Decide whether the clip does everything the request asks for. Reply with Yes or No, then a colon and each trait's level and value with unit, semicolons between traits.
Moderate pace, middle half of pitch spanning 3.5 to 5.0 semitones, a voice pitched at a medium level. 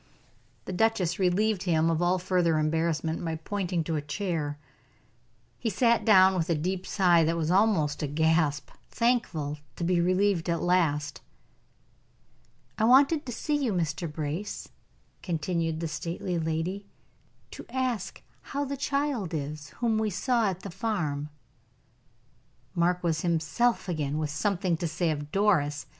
Yes: average, 150 wpm; average, 4.3 semitones; medium, 175 Hz